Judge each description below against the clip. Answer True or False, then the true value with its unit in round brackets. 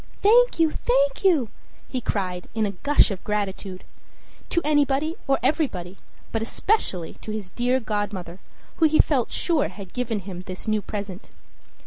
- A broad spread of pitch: True (7.5 semitones)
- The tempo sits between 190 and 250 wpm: False (155 wpm)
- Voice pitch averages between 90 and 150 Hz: False (220 Hz)